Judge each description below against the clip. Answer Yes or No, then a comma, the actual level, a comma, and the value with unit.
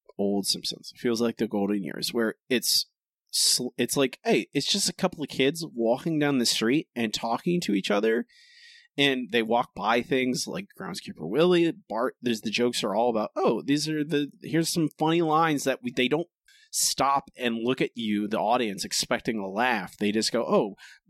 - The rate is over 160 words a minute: Yes, average, 195 wpm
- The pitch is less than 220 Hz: Yes, medium, 140 Hz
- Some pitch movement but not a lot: No, wide, 5.7 semitones